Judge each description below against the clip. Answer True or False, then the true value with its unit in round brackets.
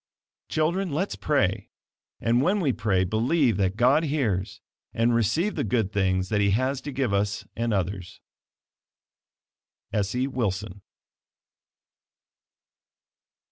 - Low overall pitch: True (115 Hz)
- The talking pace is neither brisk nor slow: False (115 wpm)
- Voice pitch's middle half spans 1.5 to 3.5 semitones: False (5.6 semitones)